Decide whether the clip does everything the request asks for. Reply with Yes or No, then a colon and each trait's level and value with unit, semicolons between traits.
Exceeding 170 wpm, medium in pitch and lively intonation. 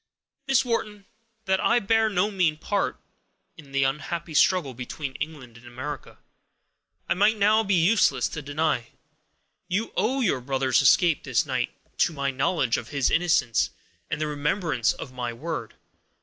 No: average, 155 wpm; medium, 155 Hz; wide, 6.4 semitones